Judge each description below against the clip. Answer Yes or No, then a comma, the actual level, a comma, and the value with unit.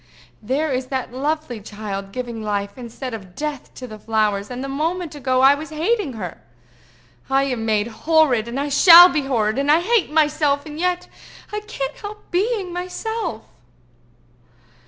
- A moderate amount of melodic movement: No, wide, 6.1 semitones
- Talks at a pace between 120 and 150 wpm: No, average, 165 wpm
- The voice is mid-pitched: No, very high, 275 Hz